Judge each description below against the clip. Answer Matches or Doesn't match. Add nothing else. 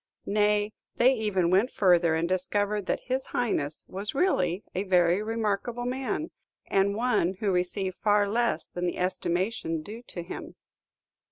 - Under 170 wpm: Matches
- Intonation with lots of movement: Doesn't match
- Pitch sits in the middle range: Doesn't match